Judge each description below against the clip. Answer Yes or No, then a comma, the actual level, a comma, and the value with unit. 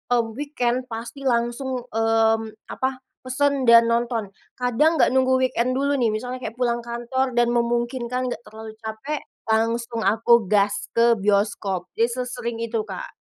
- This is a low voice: No, high, 235 Hz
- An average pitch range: No, narrow, 2.2 semitones